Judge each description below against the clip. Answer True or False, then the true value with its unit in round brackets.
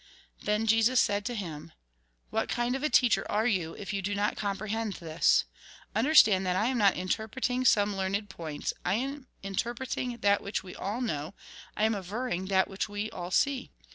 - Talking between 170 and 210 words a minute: True (190 wpm)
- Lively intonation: False (3.9 semitones)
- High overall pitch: True (205 Hz)